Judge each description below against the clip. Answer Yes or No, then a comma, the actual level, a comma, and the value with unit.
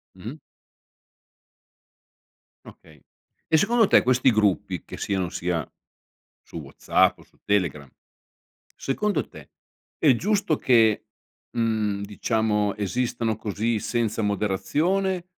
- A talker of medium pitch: No, low, 110 Hz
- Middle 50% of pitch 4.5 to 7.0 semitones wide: Yes, average, 4.8 semitones